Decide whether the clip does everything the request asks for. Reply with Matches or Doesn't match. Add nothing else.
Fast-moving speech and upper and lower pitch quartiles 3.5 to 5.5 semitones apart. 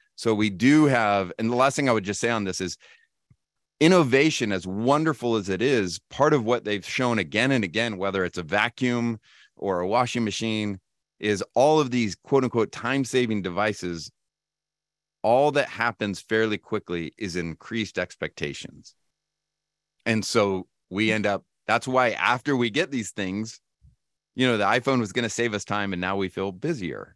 Doesn't match